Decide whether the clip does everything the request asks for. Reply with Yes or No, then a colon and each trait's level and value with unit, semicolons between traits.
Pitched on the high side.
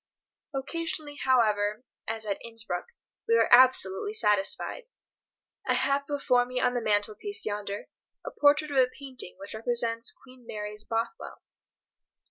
Yes: high, 245 Hz